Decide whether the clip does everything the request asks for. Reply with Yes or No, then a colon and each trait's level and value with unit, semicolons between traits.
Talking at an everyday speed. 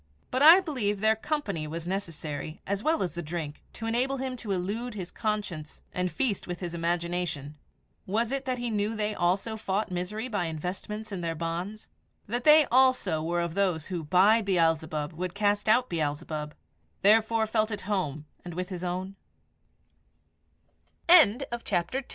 Yes: average, 150 wpm